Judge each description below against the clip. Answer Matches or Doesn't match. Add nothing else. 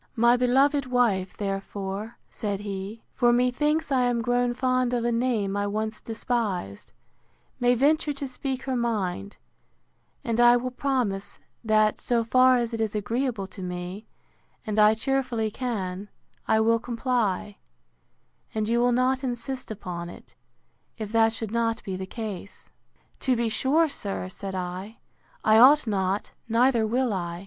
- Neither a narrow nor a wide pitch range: Matches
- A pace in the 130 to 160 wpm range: Matches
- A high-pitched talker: Matches